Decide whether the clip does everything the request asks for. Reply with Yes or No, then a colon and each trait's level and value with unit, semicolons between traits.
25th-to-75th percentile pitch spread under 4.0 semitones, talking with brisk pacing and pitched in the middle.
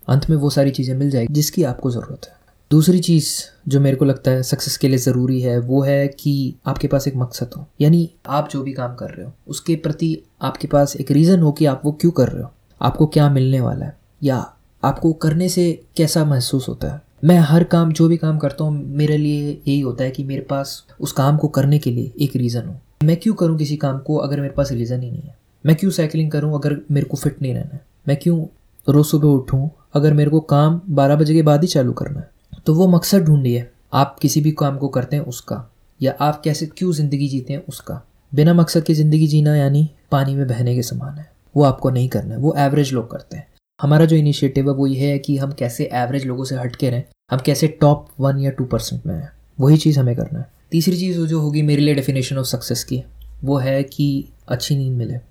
Yes: narrow, 2.5 semitones; fast, 240 wpm; medium, 145 Hz